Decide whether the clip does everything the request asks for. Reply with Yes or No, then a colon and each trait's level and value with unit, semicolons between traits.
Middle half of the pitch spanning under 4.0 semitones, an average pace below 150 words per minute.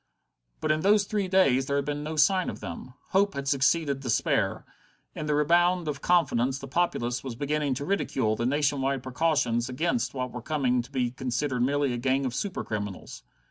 No: average, 3.6 semitones; average, 195 wpm